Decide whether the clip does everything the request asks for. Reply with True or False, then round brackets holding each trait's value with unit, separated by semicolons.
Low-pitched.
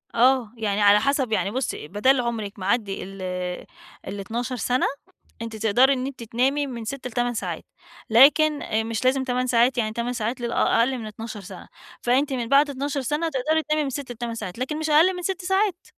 False (245 Hz)